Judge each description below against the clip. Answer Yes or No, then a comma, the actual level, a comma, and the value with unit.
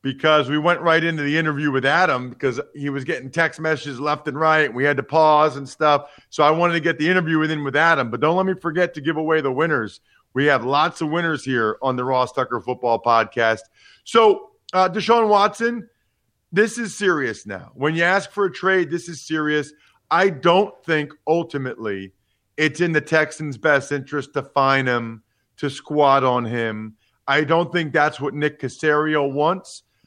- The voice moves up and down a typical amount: Yes, average, 3.6 semitones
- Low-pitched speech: No, medium, 150 Hz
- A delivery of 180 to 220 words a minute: Yes, average, 200 wpm